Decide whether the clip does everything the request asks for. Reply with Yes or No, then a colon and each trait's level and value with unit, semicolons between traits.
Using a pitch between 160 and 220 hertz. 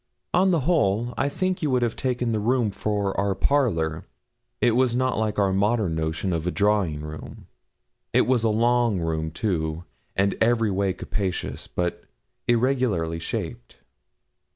No: low, 105 Hz